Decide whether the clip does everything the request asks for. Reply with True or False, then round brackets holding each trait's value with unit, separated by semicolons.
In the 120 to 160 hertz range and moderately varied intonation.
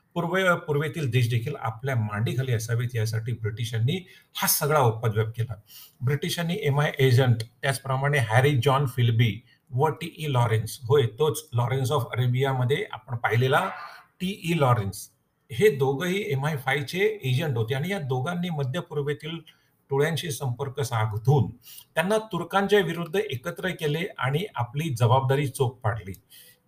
True (140 Hz; 4.4 semitones)